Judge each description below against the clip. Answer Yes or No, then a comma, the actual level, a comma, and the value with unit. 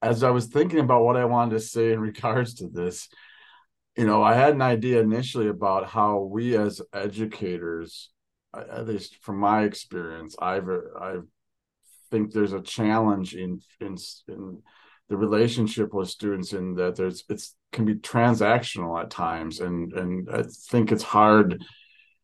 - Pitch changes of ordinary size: Yes, average, 3.9 semitones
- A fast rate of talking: No, average, 160 wpm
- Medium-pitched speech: No, low, 105 Hz